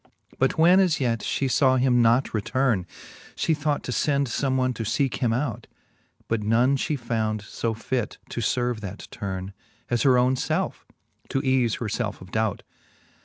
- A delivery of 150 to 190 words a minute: Yes, average, 175 wpm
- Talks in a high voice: No, low, 125 Hz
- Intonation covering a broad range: No, average, 3.2 semitones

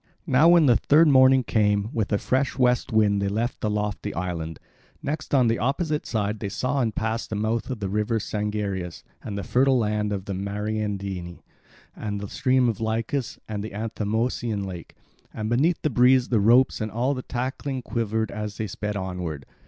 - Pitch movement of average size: Yes, average, 3.6 semitones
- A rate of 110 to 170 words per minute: No, average, 190 wpm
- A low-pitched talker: Yes, low, 110 Hz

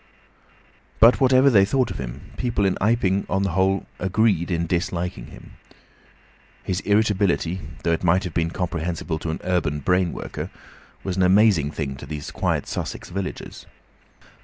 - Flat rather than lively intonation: No, average, 3.0 semitones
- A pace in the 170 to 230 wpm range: No, average, 160 wpm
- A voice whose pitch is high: No, very low, 90 Hz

